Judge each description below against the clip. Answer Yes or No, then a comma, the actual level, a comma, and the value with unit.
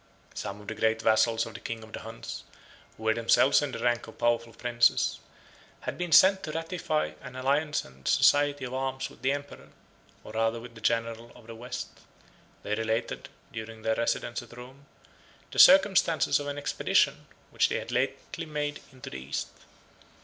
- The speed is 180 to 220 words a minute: Yes, average, 185 wpm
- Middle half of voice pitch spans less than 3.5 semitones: No, average, 4.1 semitones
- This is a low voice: Yes, low, 120 Hz